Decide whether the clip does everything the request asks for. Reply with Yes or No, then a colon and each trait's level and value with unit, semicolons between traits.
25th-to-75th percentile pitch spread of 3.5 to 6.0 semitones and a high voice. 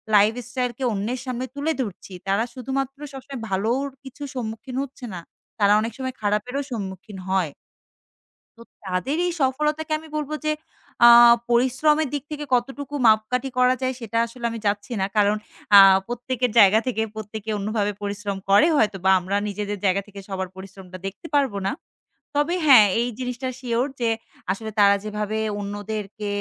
Yes: average, 4.4 semitones; high, 230 Hz